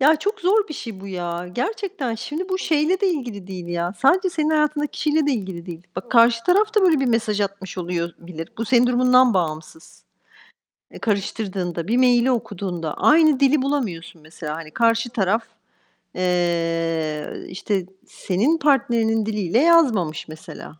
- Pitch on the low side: No, high, 225 Hz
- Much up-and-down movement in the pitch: Yes, wide, 8.7 semitones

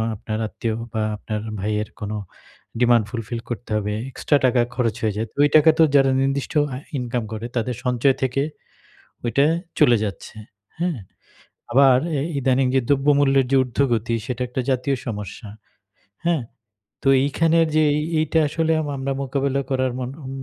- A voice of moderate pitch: No, low, 130 Hz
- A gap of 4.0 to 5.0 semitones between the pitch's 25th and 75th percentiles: No, average, 3.0 semitones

